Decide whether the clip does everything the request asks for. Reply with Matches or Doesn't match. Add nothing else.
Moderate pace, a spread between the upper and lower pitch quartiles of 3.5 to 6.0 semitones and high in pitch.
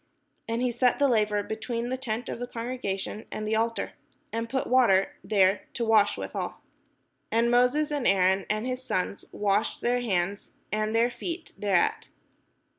Doesn't match